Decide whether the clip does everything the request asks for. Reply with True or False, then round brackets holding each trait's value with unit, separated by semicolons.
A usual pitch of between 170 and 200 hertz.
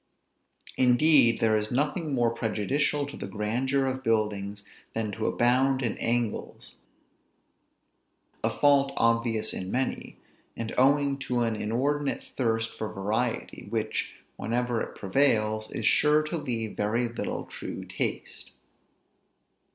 False (120 Hz)